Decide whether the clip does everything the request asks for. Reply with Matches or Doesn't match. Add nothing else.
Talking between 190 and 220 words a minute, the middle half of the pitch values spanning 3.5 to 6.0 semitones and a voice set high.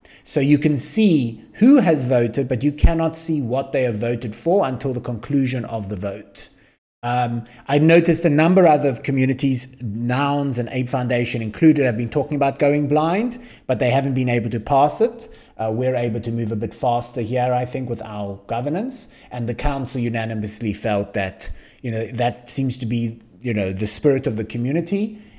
Doesn't match